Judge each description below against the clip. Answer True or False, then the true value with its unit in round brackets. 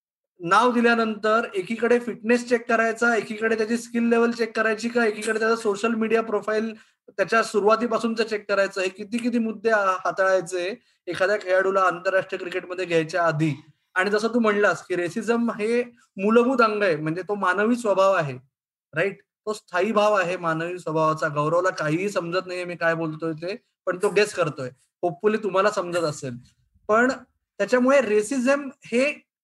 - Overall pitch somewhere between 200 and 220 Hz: True (210 Hz)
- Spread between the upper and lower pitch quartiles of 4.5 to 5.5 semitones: False (3.9 semitones)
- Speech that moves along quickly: True (155 wpm)